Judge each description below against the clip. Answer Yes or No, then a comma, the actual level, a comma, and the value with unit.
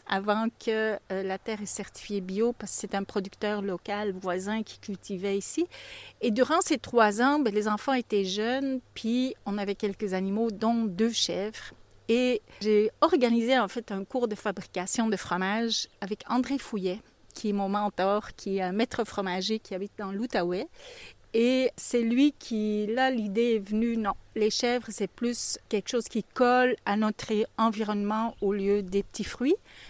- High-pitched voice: Yes, high, 215 Hz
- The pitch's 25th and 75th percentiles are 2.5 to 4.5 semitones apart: Yes, average, 2.9 semitones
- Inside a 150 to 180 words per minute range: Yes, average, 175 wpm